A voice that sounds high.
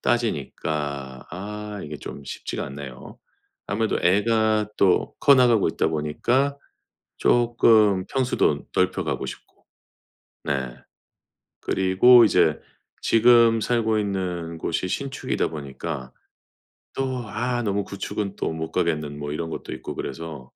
No: very low, 95 Hz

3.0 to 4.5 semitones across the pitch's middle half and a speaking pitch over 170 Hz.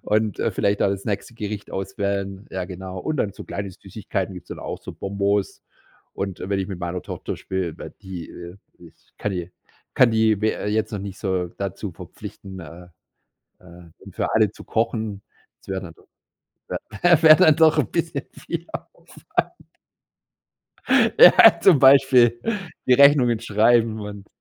No: average, 3.6 semitones; low, 100 Hz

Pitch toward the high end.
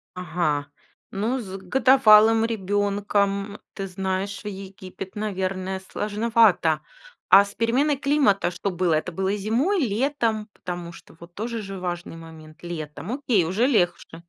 Yes: high, 195 Hz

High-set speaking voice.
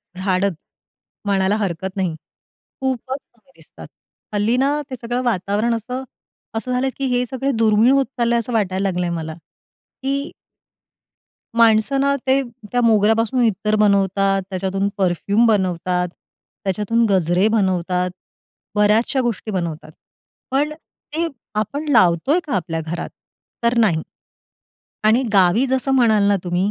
Yes: high, 210 Hz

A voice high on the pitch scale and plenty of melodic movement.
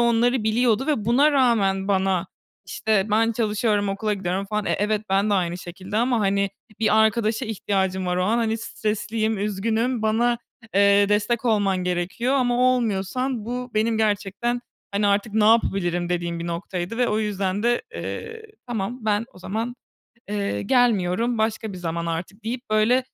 No: high, 215 Hz; average, 3.2 semitones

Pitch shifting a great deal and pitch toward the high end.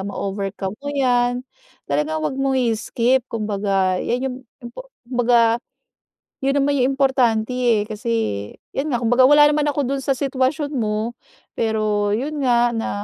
No: average, 3.9 semitones; high, 245 Hz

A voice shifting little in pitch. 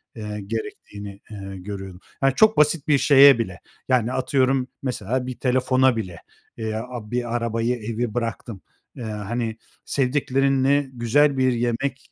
No: average, 3.4 semitones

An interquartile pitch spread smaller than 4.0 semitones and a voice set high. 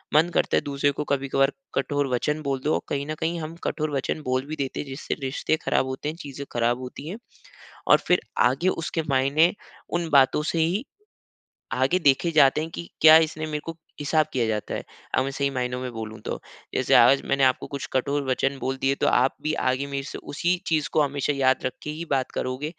No: average, 2.9 semitones; medium, 140 Hz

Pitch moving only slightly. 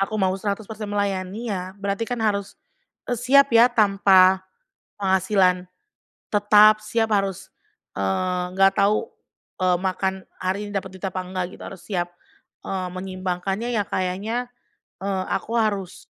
Yes: narrow, 2.3 semitones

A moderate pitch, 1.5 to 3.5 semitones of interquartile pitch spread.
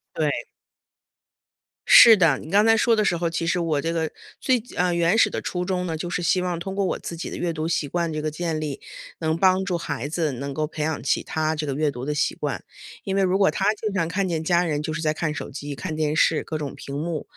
Yes: medium, 165 Hz; average, 2.8 semitones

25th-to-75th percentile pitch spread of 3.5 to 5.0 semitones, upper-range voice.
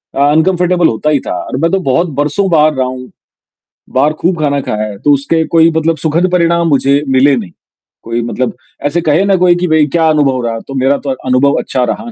No: average, 4.2 semitones; medium, 150 Hz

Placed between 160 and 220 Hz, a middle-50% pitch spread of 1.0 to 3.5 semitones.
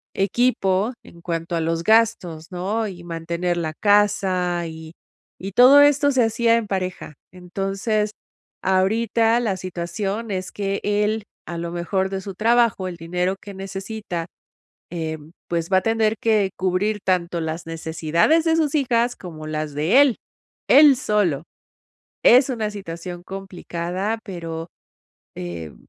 No: high, 190 Hz; average, 4.3 semitones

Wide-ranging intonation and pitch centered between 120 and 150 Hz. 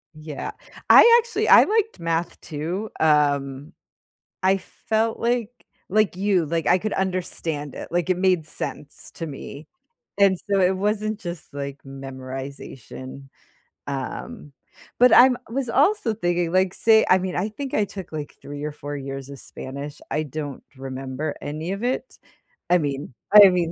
No: wide, 6.1 semitones; medium, 170 Hz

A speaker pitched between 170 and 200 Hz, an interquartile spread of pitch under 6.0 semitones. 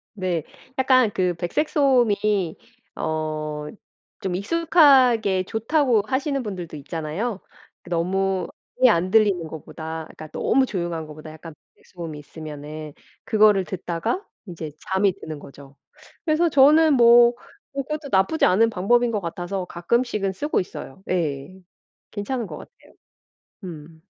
No: high, 190 Hz; wide, 6.9 semitones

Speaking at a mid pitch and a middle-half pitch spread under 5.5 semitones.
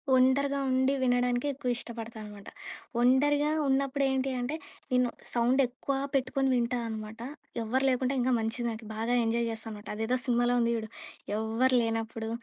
No: high, 245 Hz; narrow, 2.6 semitones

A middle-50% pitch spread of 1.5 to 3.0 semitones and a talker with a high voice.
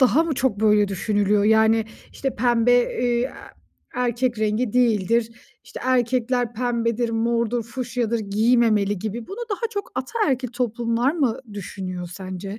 Yes: average, 2.7 semitones; high, 235 Hz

